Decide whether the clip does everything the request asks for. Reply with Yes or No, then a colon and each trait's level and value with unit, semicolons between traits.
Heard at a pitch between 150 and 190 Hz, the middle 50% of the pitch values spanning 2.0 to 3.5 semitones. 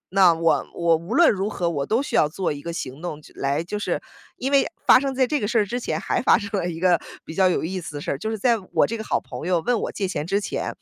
No: medium, 185 Hz; average, 5.0 semitones